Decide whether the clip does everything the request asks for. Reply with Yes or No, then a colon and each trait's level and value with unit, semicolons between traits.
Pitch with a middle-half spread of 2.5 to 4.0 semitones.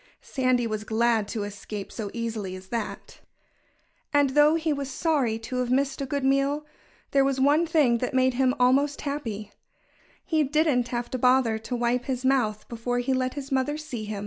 Yes: average, 3.3 semitones